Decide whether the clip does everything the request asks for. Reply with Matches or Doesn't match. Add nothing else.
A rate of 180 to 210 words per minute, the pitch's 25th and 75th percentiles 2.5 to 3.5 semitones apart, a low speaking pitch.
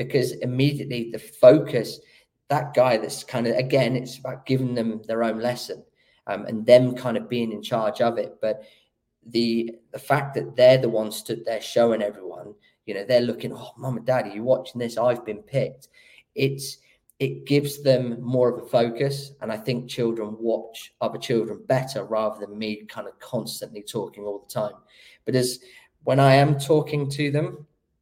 Matches